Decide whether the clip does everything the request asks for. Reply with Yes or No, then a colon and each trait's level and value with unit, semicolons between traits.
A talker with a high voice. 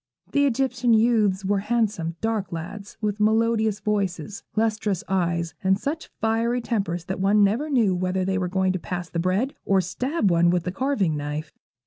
Yes: high, 200 Hz